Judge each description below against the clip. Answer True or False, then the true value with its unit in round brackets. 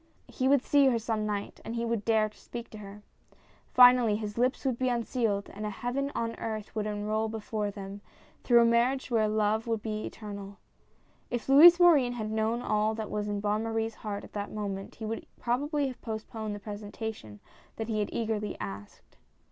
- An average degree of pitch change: False (2.2 semitones)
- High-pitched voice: True (220 Hz)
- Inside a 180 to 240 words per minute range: True (195 wpm)